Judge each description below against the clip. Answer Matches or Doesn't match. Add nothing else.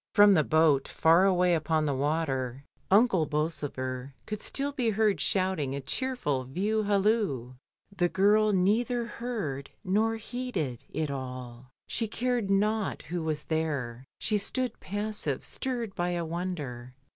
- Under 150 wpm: Doesn't match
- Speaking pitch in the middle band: Matches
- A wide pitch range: Matches